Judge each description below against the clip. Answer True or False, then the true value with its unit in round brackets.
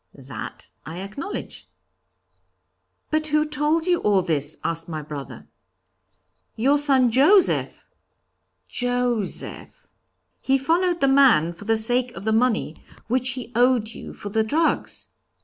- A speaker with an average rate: False (130 wpm)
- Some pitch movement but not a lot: False (5.9 semitones)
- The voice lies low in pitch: False (245 Hz)